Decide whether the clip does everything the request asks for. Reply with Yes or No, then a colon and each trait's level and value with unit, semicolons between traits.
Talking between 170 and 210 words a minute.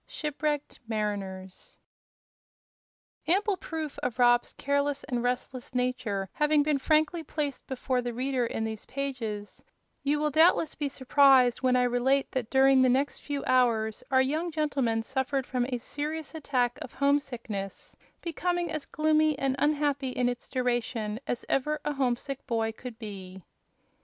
No: average, 145 wpm